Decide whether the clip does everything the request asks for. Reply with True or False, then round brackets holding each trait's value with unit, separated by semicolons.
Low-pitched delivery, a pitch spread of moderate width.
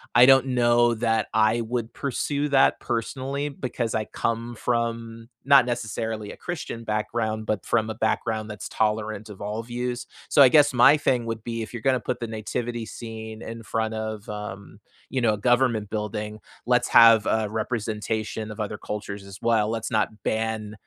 False (115 Hz; 1.9 semitones)